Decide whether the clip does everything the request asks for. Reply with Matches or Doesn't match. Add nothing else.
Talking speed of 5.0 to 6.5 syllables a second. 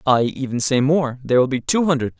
Matches